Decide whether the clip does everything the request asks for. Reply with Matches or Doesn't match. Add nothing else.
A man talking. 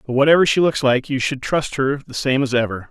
Matches